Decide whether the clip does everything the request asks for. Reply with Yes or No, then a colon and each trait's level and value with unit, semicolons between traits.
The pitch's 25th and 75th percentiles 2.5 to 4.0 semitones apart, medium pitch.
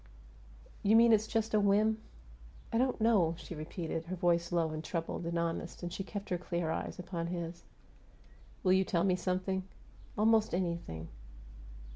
Yes: average, 3.4 semitones; medium, 180 Hz